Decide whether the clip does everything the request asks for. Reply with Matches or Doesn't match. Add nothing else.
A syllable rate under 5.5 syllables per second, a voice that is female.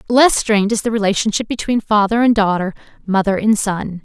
Doesn't match